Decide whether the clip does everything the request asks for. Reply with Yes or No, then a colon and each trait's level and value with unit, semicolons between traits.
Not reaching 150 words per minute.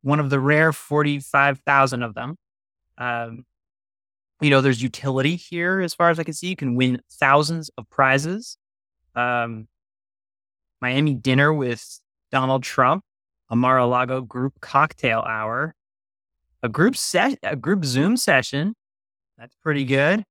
Yes: average, 140 wpm